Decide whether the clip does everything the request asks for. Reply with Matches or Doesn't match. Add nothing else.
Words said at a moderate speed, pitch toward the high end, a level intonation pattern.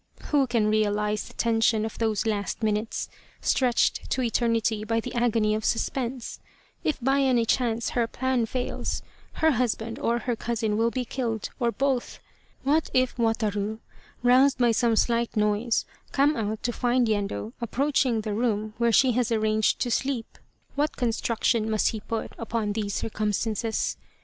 Matches